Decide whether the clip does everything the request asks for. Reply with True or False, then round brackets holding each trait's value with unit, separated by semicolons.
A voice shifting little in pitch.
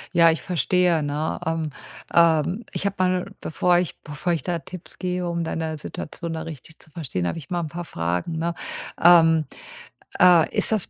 True (2.1 semitones)